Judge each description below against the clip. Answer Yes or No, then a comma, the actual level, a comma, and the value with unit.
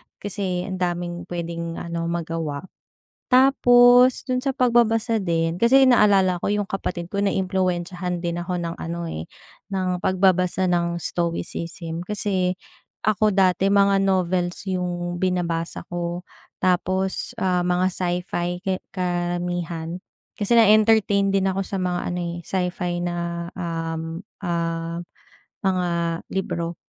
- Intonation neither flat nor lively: No, narrow, 2.1 semitones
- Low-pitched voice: No, medium, 180 Hz